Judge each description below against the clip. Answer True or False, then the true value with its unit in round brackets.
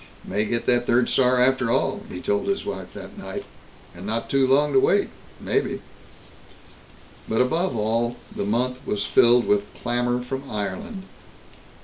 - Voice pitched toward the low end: True (125 Hz)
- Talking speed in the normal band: True (155 wpm)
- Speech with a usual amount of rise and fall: True (3.2 semitones)